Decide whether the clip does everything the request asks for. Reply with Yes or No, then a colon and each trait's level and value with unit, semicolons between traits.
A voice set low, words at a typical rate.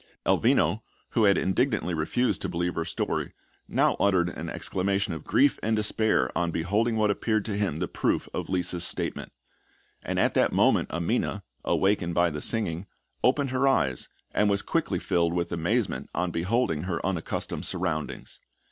Yes: very low, 95 Hz; average, 165 wpm